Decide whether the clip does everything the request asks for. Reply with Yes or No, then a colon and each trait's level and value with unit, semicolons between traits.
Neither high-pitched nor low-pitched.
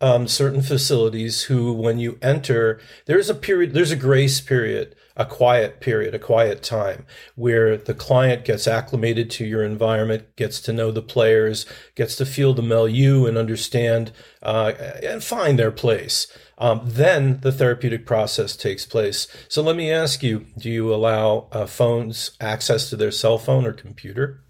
No: low, 120 Hz